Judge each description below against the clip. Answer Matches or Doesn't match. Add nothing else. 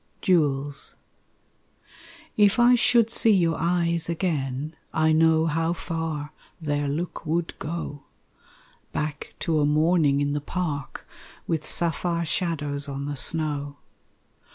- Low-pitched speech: Doesn't match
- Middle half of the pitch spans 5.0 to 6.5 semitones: Doesn't match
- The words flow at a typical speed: Doesn't match